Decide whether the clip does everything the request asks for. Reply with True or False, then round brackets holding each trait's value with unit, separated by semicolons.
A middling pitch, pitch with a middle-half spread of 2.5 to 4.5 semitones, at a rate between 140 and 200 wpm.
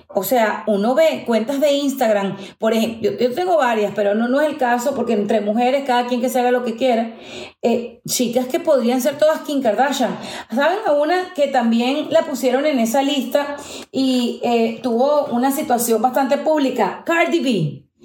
False (255 Hz; 3.8 semitones; 190 wpm)